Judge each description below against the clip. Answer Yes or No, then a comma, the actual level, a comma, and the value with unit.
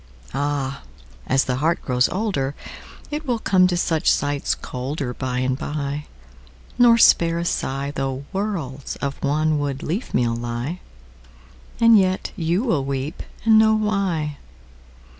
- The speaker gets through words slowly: Yes, slow, 120 wpm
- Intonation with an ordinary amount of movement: No, wide, 5.8 semitones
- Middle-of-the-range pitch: Yes, medium, 145 Hz